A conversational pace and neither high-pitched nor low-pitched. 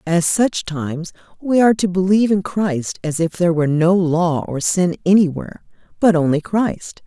Yes: average, 180 wpm; medium, 175 Hz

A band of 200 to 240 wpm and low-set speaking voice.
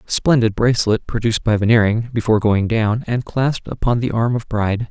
No: average, 185 wpm; low, 115 Hz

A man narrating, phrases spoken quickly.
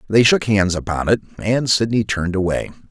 No: male; average, 185 wpm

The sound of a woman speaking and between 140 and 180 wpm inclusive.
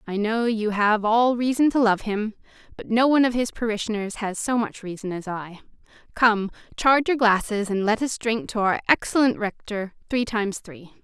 No: female; average, 190 wpm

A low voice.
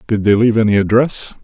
Yes: low, 110 Hz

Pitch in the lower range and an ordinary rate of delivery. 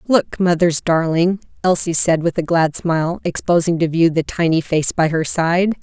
No: medium, 170 Hz; average, 185 wpm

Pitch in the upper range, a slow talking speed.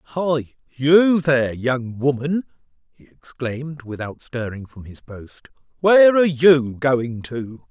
No: low, 135 Hz; slow, 130 wpm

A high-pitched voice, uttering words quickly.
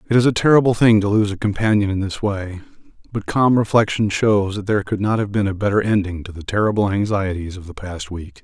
No: low, 100 Hz; fast, 235 wpm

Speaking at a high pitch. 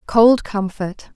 Yes: high, 210 Hz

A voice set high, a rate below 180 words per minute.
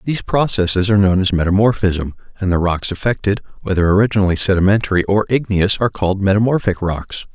No: low, 100 Hz; average, 155 wpm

